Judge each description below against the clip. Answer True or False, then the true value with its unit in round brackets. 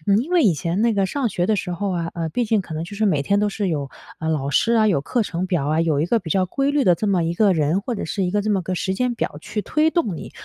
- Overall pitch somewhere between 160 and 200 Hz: True (190 Hz)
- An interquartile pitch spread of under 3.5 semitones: False (4.6 semitones)